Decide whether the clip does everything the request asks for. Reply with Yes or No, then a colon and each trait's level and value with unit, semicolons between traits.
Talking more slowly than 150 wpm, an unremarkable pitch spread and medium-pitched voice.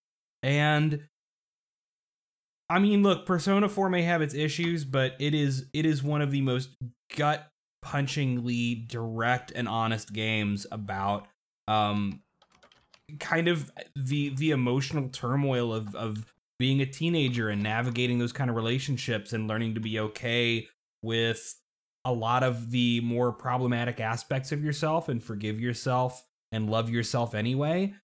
No: average, 140 wpm; average, 4.5 semitones; low, 125 Hz